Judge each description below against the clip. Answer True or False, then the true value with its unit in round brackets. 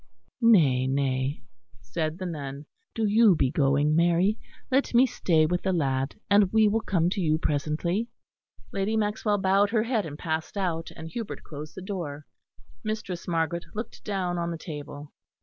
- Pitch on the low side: False (170 Hz)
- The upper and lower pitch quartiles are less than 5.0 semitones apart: False (5.4 semitones)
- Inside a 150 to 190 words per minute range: True (165 wpm)